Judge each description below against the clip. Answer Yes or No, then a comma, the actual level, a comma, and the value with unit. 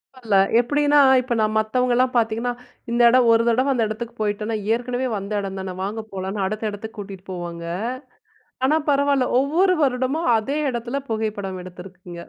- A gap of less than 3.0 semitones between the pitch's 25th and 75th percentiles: No, average, 4.2 semitones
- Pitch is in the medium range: No, high, 225 Hz